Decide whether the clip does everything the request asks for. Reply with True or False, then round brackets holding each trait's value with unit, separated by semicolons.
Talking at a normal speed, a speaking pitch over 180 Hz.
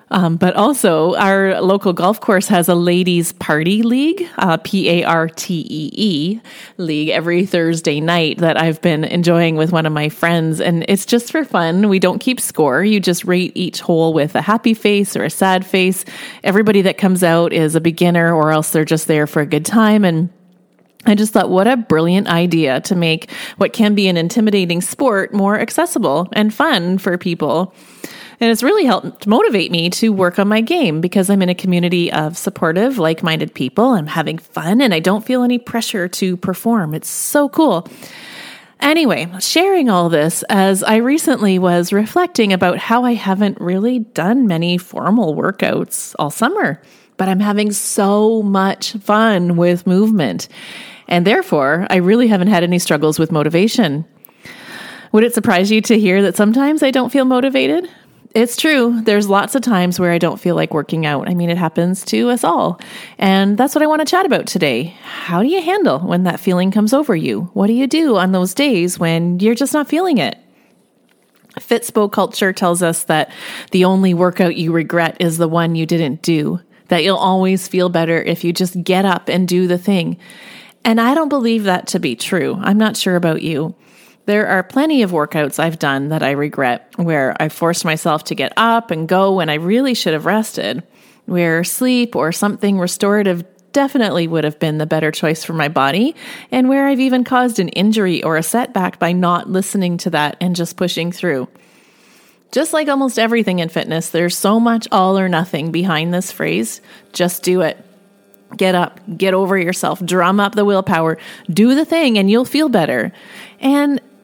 True (190 wpm; 190 Hz)